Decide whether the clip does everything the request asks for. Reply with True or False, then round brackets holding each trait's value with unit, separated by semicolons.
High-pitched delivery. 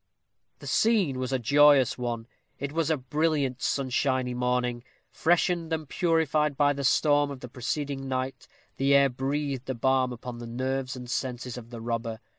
False (135 Hz)